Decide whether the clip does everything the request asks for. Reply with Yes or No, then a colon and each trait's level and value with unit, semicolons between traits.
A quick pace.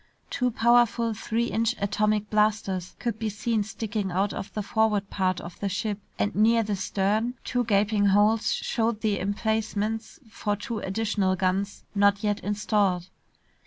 No: average, 155 wpm